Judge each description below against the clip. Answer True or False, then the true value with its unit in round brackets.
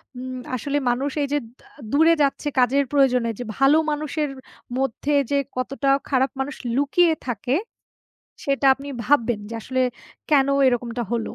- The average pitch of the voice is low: False (270 Hz)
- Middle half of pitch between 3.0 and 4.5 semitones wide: False (2.4 semitones)